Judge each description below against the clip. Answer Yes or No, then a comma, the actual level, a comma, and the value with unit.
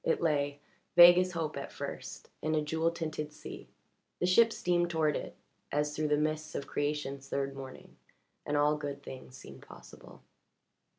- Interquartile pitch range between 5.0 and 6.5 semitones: No, narrow, 2.4 semitones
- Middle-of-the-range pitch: Yes, medium, 150 Hz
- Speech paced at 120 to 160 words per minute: No, average, 170 wpm